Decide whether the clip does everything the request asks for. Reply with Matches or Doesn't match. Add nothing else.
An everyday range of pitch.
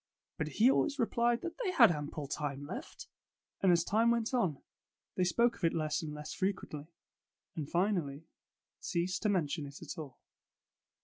Doesn't match